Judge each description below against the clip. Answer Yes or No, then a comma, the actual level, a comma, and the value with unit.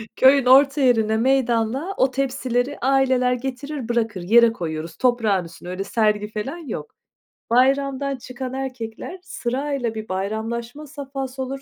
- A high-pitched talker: Yes, very high, 250 Hz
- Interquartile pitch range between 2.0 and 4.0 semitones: Yes, average, 3.4 semitones